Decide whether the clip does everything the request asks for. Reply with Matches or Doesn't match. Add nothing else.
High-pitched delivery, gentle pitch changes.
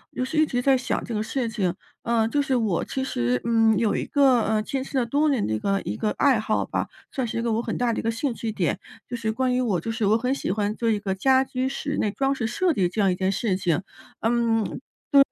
Doesn't match